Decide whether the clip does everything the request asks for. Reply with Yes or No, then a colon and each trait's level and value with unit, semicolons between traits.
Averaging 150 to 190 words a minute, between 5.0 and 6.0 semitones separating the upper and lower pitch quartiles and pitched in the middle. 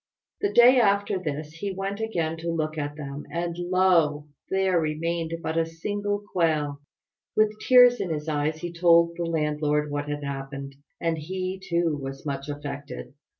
No: average, 165 wpm; average, 3.9 semitones; medium, 165 Hz